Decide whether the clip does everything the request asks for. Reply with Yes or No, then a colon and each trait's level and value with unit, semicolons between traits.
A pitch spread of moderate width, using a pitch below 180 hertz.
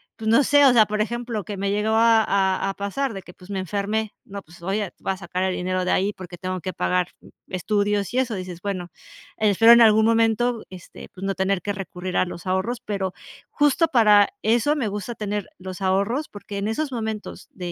No: average, 3.1 semitones; high, 205 Hz